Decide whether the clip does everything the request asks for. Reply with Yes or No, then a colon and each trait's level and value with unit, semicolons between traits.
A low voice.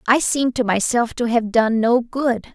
No: high, 235 Hz